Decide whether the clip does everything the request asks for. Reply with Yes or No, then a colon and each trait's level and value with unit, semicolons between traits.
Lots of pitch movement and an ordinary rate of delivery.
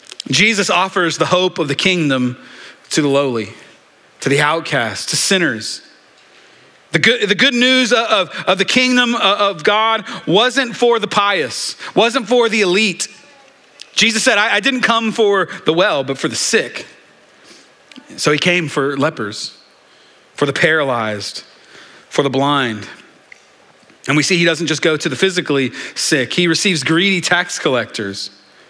Yes: wide, 6.9 semitones; average, 160 wpm